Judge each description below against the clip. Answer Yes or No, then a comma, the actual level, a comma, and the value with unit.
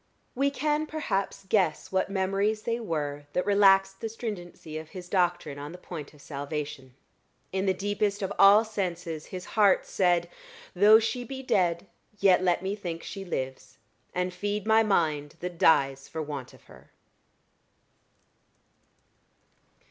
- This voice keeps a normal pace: Yes, average, 150 wpm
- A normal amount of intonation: Yes, average, 4.1 semitones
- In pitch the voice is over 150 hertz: Yes, medium, 185 Hz